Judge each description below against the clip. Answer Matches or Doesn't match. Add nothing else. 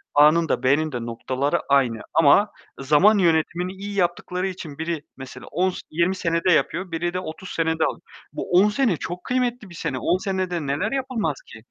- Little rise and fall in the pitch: Doesn't match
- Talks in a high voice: Doesn't match